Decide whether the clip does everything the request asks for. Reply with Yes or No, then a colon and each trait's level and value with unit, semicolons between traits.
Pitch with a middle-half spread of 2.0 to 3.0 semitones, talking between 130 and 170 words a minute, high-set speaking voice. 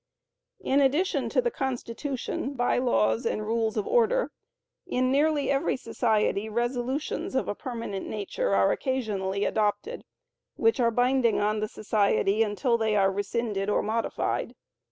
No: average, 4.2 semitones; average, 140 wpm; high, 235 Hz